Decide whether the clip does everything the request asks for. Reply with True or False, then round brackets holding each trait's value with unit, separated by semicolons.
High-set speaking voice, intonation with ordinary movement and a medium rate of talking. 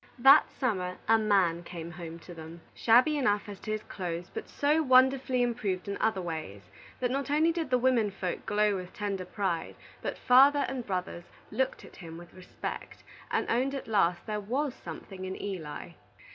False (205 Hz; 6.0 semitones; 185 wpm)